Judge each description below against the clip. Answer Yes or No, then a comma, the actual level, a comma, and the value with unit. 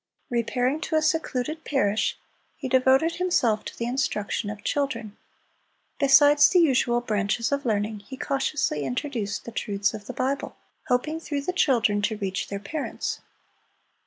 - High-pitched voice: Yes, very high, 250 Hz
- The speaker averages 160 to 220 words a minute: No, average, 150 wpm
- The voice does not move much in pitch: No, wide, 5.4 semitones